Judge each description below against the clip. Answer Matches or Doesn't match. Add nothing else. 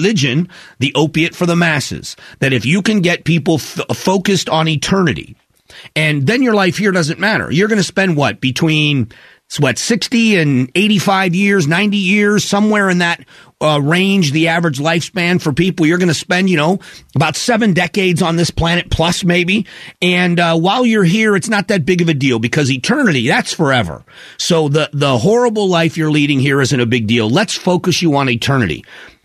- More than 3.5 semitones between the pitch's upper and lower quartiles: Matches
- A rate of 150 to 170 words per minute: Doesn't match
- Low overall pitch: Doesn't match